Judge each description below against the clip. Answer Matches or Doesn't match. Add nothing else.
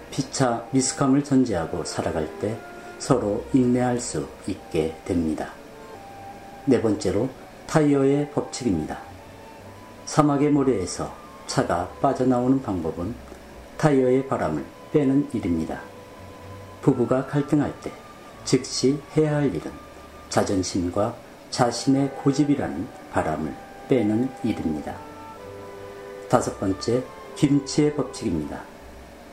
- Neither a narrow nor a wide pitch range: Doesn't match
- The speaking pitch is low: Matches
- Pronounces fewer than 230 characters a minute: Doesn't match